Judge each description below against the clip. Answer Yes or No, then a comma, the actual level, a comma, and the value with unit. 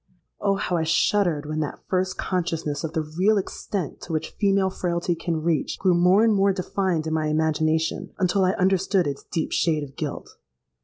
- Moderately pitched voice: Yes, medium, 175 Hz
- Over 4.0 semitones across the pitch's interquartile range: No, average, 3.3 semitones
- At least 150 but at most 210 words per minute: Yes, average, 190 wpm